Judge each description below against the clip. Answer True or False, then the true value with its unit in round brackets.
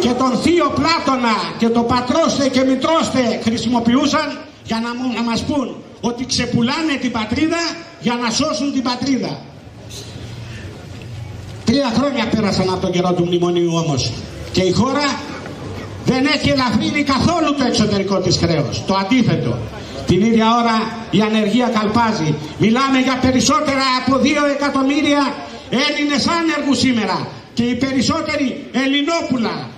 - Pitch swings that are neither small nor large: False (6.8 semitones)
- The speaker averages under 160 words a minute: True (130 wpm)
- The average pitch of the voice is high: True (240 Hz)